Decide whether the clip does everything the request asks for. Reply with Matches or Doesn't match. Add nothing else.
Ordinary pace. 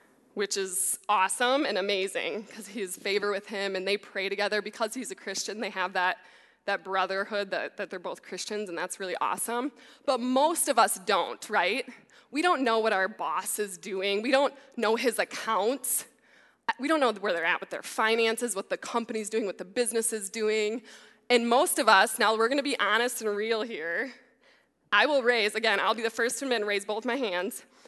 Doesn't match